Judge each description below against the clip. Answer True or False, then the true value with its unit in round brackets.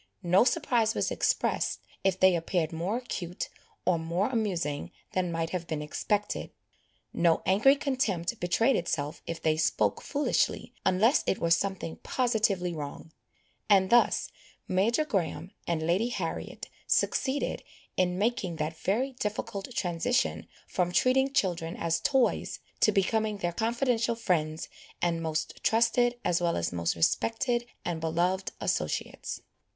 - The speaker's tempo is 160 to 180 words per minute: False (135 wpm)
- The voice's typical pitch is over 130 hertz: True (185 Hz)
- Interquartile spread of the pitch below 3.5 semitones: False (5.5 semitones)